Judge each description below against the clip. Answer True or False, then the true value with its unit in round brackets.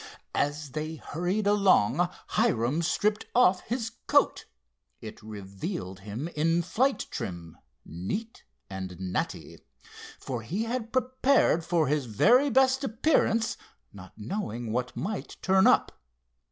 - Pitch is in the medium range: True (165 Hz)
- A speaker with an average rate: False (120 wpm)